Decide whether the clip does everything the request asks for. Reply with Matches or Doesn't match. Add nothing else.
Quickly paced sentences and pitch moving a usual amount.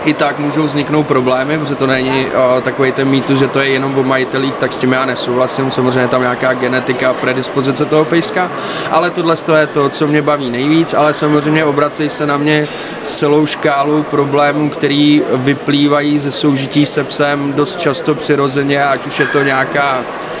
Doesn't match